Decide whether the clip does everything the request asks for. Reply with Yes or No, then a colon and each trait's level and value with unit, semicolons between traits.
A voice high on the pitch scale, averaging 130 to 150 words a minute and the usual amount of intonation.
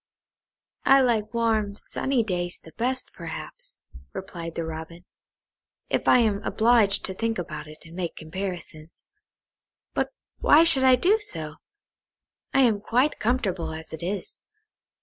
No: high, 200 Hz; average, 140 wpm; wide, 6.4 semitones